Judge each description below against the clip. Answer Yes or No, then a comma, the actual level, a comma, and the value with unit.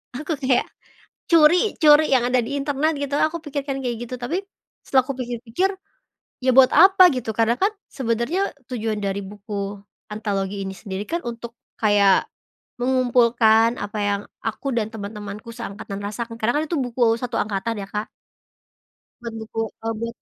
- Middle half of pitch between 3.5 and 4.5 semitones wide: Yes, average, 4.0 semitones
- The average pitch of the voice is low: No, high, 235 Hz